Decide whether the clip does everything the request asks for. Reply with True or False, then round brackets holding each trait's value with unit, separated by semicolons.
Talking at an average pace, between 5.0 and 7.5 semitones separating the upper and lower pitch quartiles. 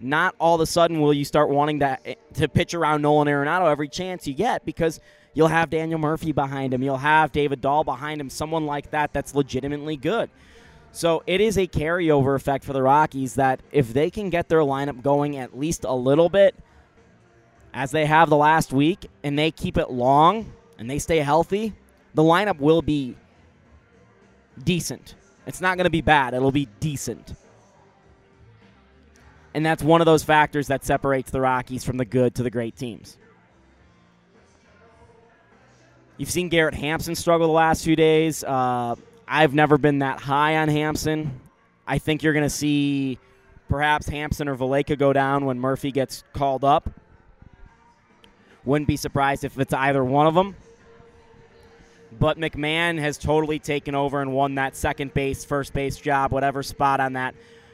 False (175 wpm; 2.6 semitones)